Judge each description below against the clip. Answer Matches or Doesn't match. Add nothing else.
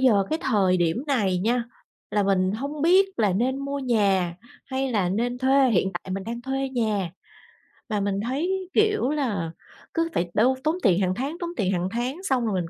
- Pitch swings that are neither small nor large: Doesn't match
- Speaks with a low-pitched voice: Doesn't match